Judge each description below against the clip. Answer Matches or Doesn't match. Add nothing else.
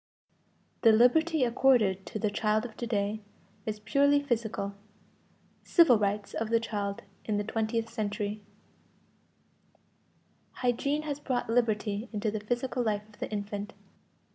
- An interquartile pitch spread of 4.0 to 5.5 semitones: Doesn't match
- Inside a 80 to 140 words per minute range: Matches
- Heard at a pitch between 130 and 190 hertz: Doesn't match